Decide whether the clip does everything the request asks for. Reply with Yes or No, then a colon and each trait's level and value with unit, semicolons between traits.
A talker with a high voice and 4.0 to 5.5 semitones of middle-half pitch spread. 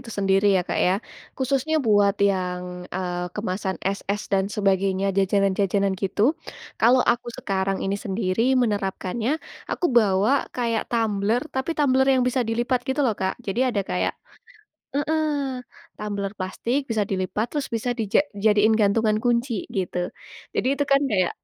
Yes: high, 210 Hz; average, 4.3 semitones